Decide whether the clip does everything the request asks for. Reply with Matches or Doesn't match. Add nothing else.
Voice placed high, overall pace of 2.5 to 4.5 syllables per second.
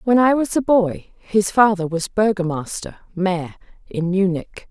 Matches